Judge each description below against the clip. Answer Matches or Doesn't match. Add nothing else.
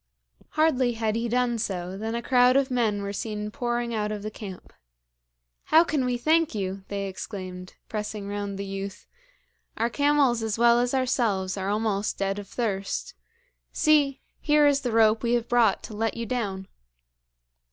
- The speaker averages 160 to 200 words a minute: Matches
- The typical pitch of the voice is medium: Doesn't match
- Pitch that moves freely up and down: Doesn't match